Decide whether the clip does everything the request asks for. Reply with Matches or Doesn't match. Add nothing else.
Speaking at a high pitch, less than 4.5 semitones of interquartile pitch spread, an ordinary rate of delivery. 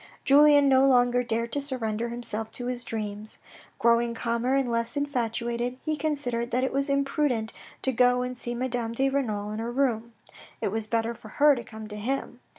Matches